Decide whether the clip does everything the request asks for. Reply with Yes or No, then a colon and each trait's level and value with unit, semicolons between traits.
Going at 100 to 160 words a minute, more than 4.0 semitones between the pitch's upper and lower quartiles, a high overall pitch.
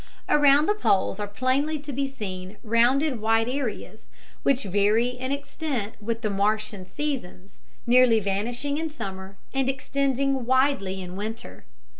Yes: average, 140 wpm; average, 5.1 semitones; high, 240 Hz